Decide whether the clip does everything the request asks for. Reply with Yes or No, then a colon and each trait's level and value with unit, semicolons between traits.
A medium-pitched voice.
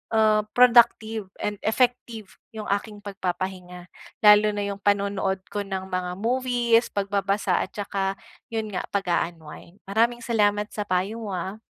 No: high, 205 Hz